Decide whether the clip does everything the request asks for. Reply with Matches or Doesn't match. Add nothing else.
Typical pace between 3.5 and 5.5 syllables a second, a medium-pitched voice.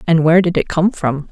Doesn't match